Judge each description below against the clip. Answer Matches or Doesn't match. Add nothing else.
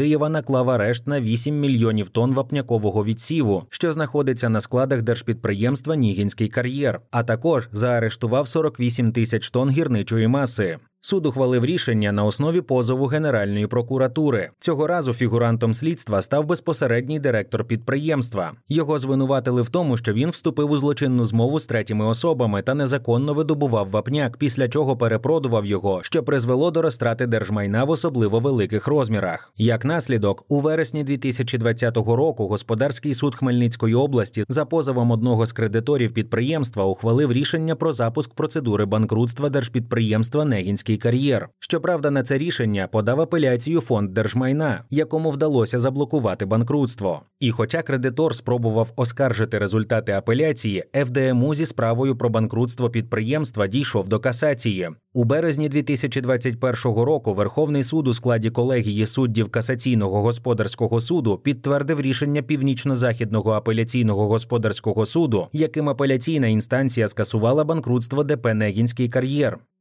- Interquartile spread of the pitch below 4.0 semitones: Doesn't match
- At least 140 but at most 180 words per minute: Doesn't match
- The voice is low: Matches